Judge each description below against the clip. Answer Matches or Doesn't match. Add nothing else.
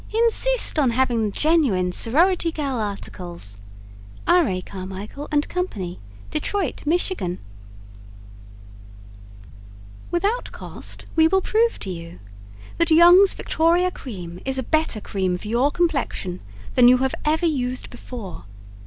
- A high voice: Matches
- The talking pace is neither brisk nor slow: Doesn't match